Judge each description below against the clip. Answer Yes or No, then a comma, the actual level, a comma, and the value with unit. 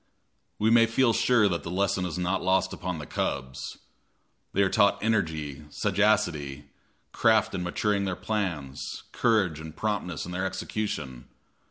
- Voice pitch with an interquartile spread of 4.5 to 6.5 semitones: Yes, average, 5.0 semitones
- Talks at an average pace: Yes, average, 150 wpm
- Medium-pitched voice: No, very low, 95 Hz